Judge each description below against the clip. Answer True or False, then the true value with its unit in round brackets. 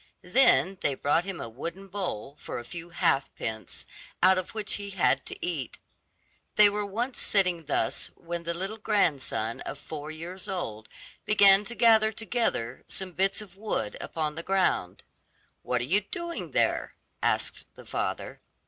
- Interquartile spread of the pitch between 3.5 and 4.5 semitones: False (5.1 semitones)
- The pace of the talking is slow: False (165 wpm)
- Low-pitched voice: False (185 Hz)